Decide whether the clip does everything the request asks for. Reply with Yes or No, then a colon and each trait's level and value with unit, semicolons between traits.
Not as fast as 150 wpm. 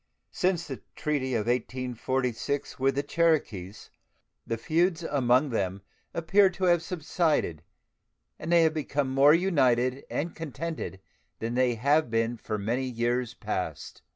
Yes: slow, 135 wpm